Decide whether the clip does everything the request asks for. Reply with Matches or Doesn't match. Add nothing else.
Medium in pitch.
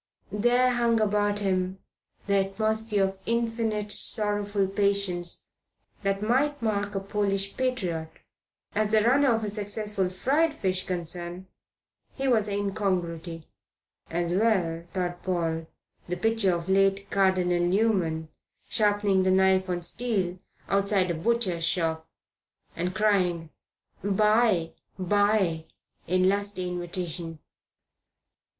Doesn't match